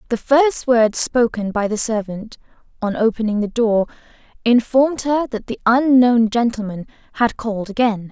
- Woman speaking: Yes, female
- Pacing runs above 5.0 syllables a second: No, 4.8 syllables/s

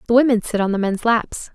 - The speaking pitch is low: No, high, 225 Hz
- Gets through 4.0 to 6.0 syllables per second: Yes, 5.9 syllables/s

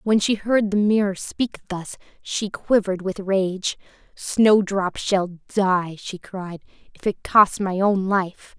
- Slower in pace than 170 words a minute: Yes, average, 155 wpm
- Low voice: No, high, 195 Hz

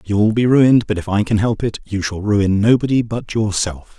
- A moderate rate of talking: No, fast, 225 wpm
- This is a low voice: Yes, low, 105 Hz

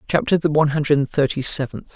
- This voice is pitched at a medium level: Yes, medium, 145 Hz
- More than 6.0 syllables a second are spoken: Yes, 6.7 syllables/s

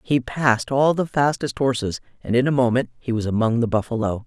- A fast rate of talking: Yes, fast, 210 wpm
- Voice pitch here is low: Yes, low, 125 Hz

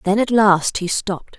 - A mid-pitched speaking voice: No, high, 200 Hz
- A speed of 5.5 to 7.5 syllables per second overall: No, 4.7 syllables/s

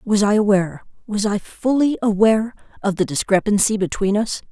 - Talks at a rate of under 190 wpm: Yes, average, 145 wpm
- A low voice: No, high, 205 Hz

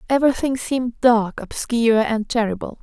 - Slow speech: Yes, slow, 125 wpm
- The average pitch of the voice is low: No, high, 235 Hz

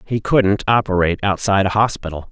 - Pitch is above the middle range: No, low, 100 Hz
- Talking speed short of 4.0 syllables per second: No, 6.1 syllables/s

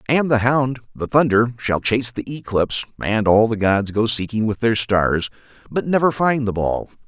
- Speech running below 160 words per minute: No, average, 195 wpm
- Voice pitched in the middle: No, low, 115 Hz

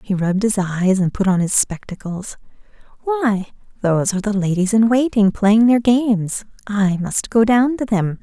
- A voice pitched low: No, high, 210 Hz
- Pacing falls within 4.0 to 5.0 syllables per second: Yes, 4.8 syllables/s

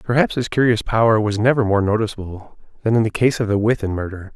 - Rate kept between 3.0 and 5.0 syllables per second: No, 6.3 syllables/s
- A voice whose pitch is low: Yes, low, 110 Hz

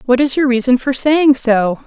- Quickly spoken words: Yes, fast, 225 wpm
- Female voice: Yes, female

